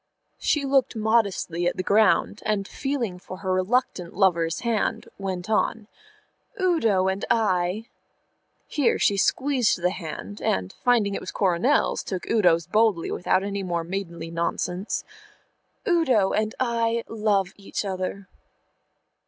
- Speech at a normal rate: No, slow, 130 wpm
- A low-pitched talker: No, high, 200 Hz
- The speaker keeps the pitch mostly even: No, average, 4.0 semitones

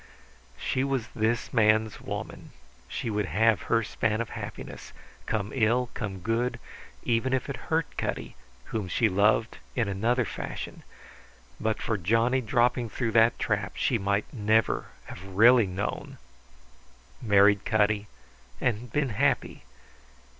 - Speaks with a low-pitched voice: Yes, low, 110 Hz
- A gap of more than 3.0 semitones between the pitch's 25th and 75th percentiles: No, narrow, 2.5 semitones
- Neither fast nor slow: No, slow, 130 wpm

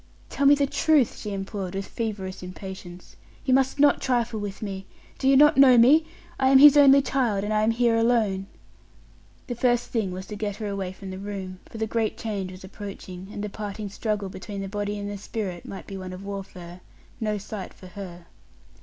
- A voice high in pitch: Yes, high, 205 Hz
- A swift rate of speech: Yes, fast, 210 wpm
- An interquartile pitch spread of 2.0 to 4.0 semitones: Yes, average, 3.7 semitones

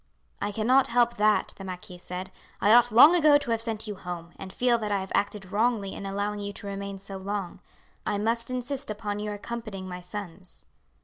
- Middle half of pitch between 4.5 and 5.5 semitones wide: No, average, 3.1 semitones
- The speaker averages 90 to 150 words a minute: No, fast, 205 wpm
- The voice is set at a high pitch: Yes, high, 205 Hz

